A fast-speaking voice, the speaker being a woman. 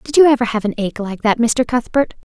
Yes: fast, 250 wpm; female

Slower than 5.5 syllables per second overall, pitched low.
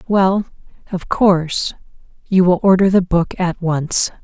No: 3.9 syllables/s; medium, 180 Hz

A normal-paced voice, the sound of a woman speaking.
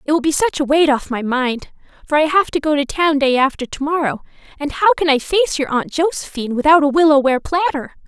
No: fast, 240 wpm; female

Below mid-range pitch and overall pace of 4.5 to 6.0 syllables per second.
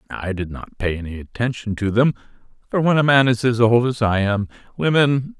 Yes: low, 115 Hz; 5.4 syllables/s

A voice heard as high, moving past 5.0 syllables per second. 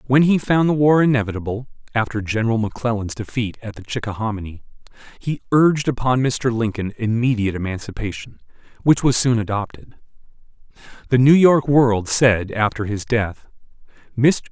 No: low, 120 Hz; 5.5 syllables/s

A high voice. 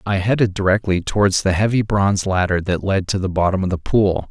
No: very low, 95 Hz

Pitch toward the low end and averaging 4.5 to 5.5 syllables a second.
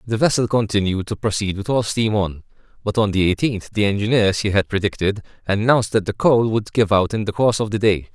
No: low, 105 Hz; 6.0 syllables/s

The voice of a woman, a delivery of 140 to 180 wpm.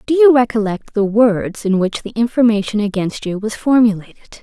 Yes: female; average, 175 wpm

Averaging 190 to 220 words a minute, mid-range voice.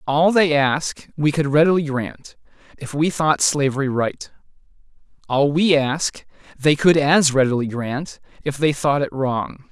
No: average, 155 wpm; medium, 145 Hz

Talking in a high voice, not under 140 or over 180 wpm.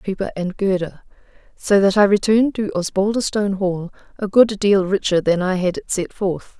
Yes: high, 200 Hz; average, 175 wpm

